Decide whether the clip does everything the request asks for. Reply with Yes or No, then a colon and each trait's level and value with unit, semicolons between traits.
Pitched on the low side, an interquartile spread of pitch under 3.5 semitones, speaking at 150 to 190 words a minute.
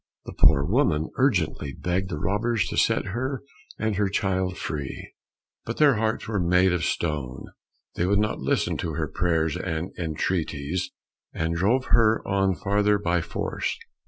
No: very low, 95 Hz; average, 4.2 semitones; average, 160 wpm